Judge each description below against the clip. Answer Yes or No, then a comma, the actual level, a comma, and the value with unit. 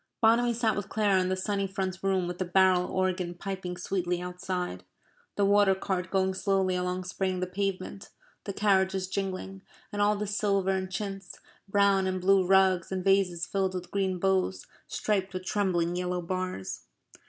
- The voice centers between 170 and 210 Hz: Yes, high, 190 Hz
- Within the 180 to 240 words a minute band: No, average, 170 wpm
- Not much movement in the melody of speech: Yes, narrow, 1.3 semitones